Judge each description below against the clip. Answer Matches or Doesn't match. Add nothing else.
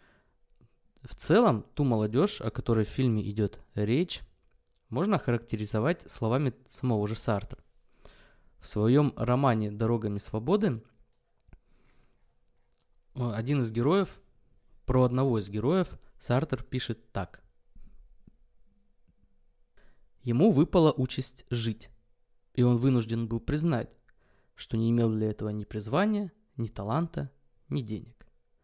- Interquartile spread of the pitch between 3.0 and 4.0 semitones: Matches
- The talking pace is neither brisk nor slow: Doesn't match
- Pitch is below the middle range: Matches